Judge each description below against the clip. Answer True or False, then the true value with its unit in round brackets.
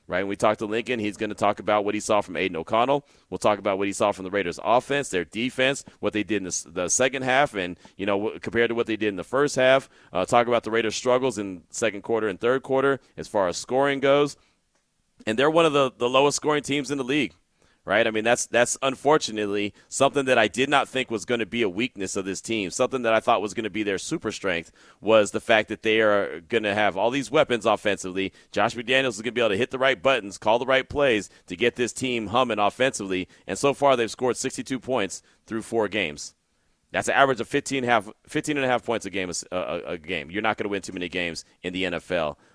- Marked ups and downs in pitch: False (4.3 semitones)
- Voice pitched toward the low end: True (115 Hz)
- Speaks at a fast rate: True (260 wpm)